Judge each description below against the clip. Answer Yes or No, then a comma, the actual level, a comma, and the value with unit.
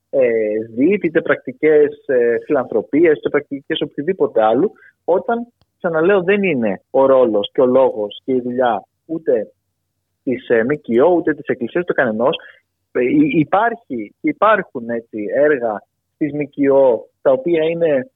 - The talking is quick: No, average, 130 wpm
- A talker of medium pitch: Yes, medium, 165 Hz